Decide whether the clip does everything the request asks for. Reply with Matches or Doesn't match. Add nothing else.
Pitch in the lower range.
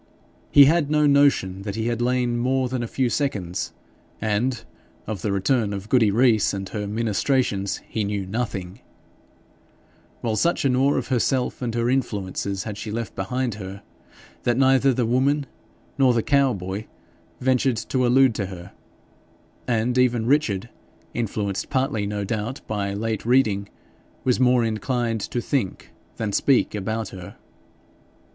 Matches